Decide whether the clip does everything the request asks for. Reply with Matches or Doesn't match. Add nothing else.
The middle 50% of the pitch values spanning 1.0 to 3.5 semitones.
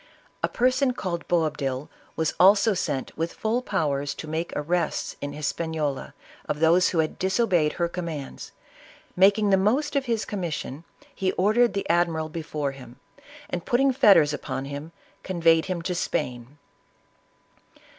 Doesn't match